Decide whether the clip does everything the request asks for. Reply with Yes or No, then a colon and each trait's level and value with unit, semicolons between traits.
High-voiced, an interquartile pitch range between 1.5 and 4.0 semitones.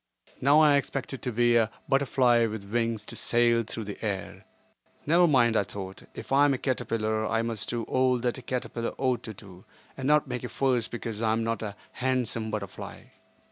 No: low, 120 Hz; average, 2.9 semitones